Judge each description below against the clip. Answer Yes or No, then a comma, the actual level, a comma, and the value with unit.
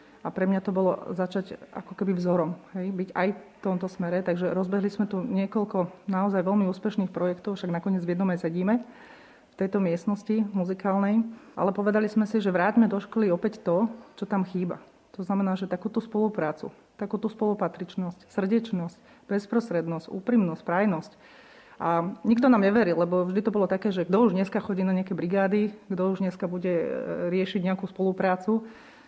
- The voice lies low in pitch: No, high, 195 Hz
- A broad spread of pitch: No, average, 2.7 semitones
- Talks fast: Yes, fast, 170 wpm